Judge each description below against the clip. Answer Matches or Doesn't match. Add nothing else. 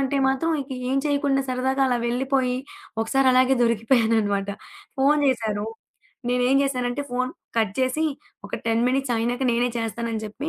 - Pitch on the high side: Matches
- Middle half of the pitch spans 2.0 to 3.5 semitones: Matches